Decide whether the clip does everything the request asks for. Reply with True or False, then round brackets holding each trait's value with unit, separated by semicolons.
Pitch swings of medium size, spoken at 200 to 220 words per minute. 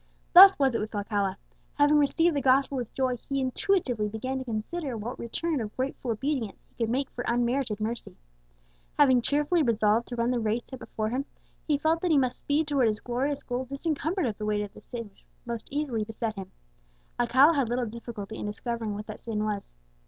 True (4.2 semitones; 205 wpm)